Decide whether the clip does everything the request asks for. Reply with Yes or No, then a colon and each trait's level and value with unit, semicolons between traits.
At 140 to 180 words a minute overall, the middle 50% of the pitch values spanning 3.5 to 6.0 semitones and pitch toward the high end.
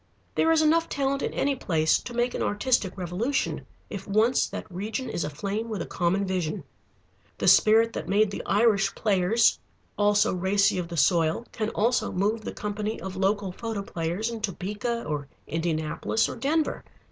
Yes: average, 170 wpm; average, 4.1 semitones; high, 205 Hz